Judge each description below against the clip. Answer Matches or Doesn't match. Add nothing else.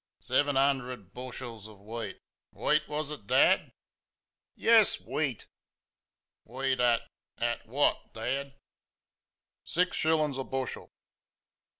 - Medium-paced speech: Doesn't match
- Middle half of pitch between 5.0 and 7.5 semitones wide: Doesn't match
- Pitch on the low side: Matches